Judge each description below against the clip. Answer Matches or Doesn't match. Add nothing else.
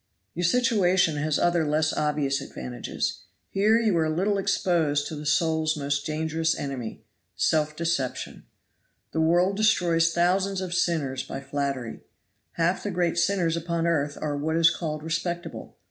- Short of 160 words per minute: Matches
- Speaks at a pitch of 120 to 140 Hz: Doesn't match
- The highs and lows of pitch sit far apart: Doesn't match